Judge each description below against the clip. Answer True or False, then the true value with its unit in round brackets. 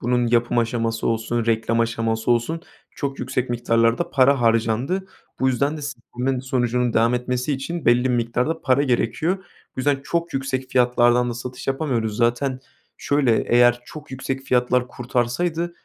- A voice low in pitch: True (125 Hz)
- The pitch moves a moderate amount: False (2.3 semitones)